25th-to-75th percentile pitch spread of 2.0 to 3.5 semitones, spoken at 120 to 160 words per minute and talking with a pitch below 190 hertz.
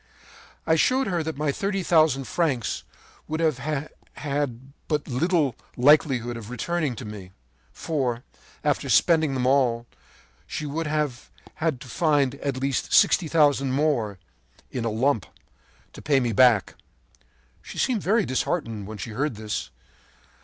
No: average, 4.3 semitones; average, 140 wpm; medium, 140 Hz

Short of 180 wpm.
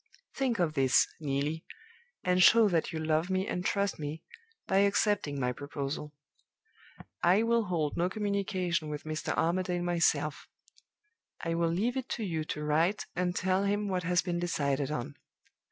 Yes: average, 160 wpm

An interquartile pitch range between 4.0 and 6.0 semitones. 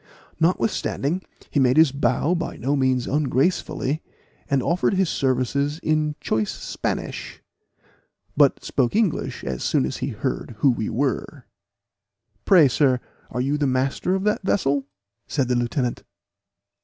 No: average, 3.6 semitones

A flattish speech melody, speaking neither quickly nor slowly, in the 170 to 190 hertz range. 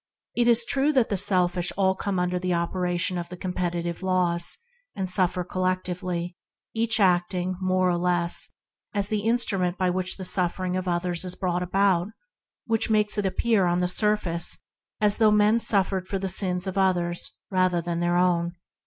Yes: narrow, 2.0 semitones; average, 180 wpm; medium, 185 Hz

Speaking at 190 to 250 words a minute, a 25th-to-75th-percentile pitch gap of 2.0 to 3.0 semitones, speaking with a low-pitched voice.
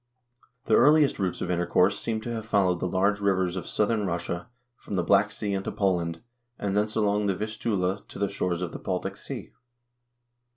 Yes: average, 195 wpm; average, 2.7 semitones; low, 100 Hz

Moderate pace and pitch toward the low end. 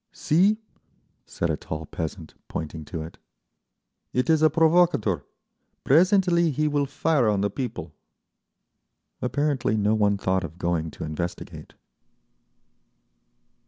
No: slow, 120 wpm; low, 110 Hz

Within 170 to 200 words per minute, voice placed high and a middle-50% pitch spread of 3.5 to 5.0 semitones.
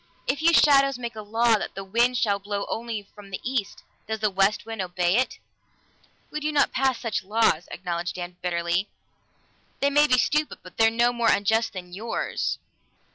Yes: average, 185 wpm; high, 220 Hz; average, 4.1 semitones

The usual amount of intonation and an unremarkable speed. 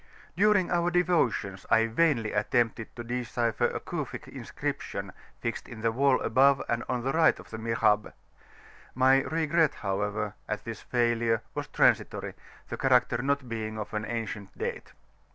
Yes: average, 3.7 semitones; average, 150 wpm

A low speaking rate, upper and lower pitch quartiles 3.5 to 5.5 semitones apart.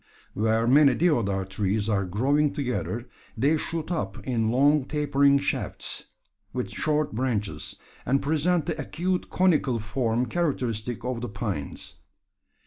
Yes: slow, 130 wpm; average, 5.2 semitones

